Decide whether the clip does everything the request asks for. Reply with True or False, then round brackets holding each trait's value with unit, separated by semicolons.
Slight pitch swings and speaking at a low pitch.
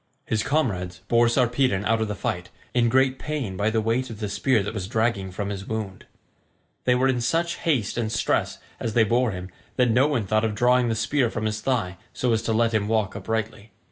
False (3.1 semitones; 115 Hz)